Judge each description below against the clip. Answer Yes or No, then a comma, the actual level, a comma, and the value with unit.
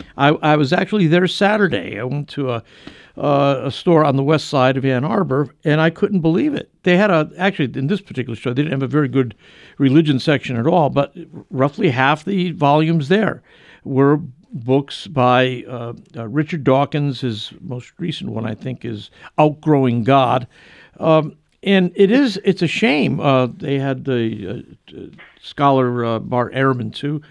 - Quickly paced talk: No, average, 180 wpm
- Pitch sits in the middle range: Yes, medium, 145 Hz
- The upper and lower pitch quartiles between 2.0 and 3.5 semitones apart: No, average, 4.6 semitones